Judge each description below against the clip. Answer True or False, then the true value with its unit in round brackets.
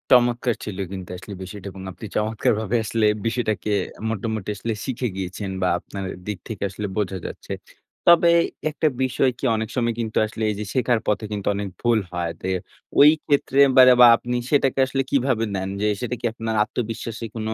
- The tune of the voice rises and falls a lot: False (3.2 semitones)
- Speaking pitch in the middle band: False (110 Hz)